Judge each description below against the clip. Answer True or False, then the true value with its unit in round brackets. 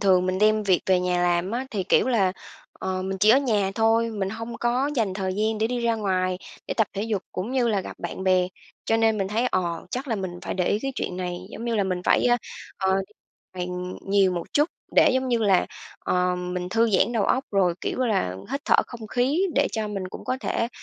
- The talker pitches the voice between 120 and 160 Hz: False (205 Hz)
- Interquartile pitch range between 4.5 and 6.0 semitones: False (3.9 semitones)